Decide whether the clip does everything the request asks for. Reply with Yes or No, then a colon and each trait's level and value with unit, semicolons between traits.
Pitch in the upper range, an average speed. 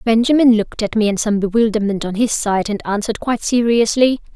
Yes: high, 220 Hz; average, 195 wpm